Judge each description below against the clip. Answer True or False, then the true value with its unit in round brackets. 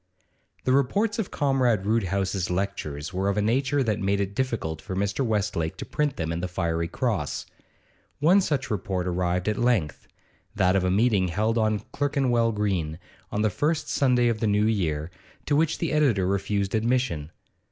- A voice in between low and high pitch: False (105 Hz)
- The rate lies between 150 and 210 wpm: True (175 wpm)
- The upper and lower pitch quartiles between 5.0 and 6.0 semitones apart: True (5.5 semitones)